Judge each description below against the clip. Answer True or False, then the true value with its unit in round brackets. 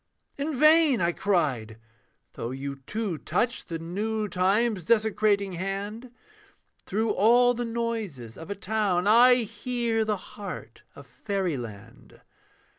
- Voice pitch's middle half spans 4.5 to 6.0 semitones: True (4.8 semitones)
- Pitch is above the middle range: True (205 Hz)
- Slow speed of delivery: True (120 wpm)